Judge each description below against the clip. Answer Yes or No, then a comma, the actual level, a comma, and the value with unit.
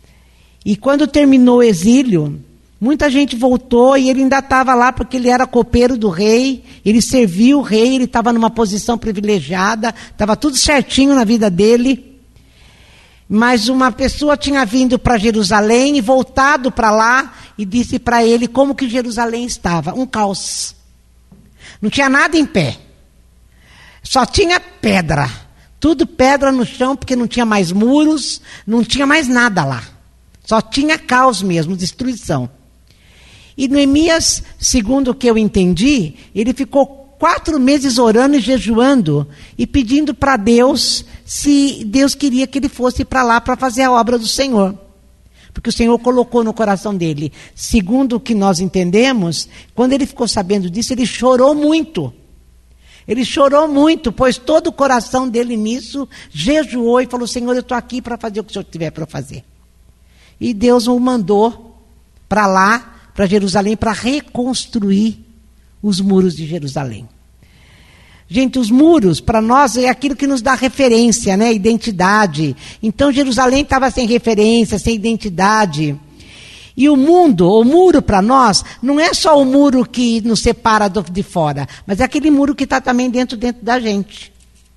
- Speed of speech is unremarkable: Yes, average, 155 wpm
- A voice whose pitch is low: No, high, 240 Hz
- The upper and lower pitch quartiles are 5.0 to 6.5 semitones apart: No, average, 4.3 semitones